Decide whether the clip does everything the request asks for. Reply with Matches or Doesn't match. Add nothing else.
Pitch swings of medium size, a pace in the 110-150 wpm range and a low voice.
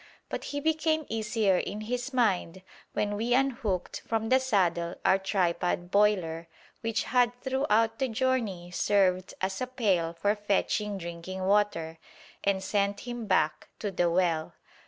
Doesn't match